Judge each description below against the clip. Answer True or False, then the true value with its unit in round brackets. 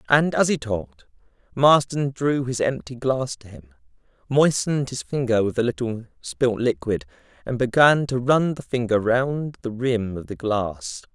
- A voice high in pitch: False (125 Hz)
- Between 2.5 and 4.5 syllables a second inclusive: True (4.4 syllables/s)